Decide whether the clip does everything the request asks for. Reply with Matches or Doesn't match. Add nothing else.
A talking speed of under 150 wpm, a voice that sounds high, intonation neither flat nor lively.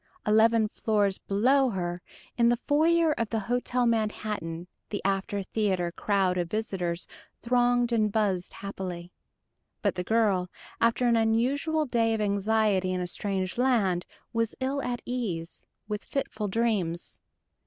Matches